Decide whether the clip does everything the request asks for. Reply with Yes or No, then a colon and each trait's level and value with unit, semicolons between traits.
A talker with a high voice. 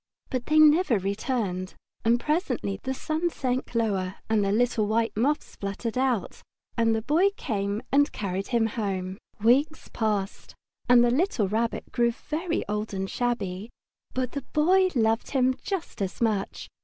Yes: high, 230 Hz